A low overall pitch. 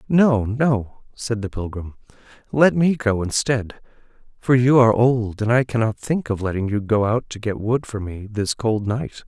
Yes: low, 115 Hz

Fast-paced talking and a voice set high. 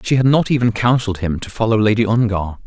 No: fast, 225 wpm; low, 110 Hz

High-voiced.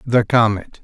No: low, 115 Hz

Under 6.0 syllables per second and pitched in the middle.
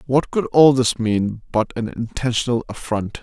No: 4.5 syllables/s; low, 120 Hz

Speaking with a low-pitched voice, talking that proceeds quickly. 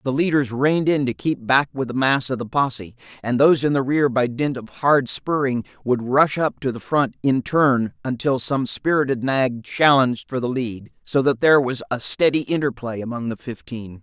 Yes: low, 130 Hz; fast, 210 wpm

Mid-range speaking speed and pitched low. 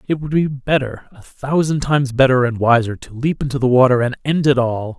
No: fast, 230 wpm; low, 130 Hz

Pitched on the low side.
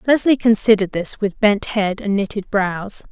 No: high, 205 Hz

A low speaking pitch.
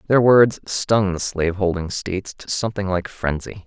Yes: very low, 95 Hz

